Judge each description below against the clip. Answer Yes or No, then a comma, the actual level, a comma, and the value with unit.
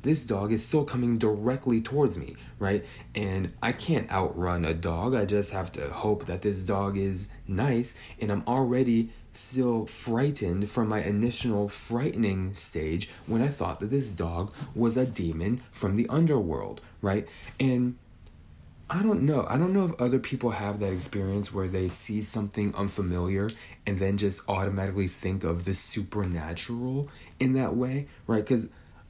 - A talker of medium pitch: No, low, 105 Hz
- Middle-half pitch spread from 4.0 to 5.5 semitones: Yes, average, 4.4 semitones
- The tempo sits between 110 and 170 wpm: Yes, average, 165 wpm